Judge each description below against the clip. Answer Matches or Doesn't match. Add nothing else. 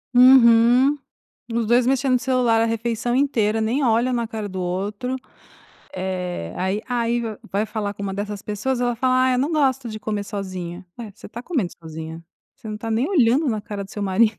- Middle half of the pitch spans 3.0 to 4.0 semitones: Matches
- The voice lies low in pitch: Doesn't match